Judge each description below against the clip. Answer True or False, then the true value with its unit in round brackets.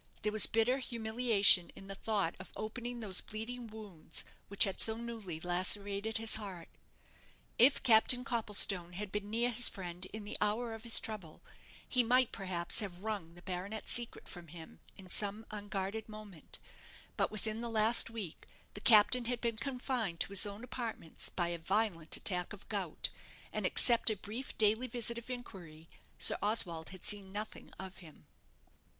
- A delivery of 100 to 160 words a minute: False (170 wpm)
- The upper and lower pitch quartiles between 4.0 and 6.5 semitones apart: False (3.4 semitones)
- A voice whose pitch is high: True (210 Hz)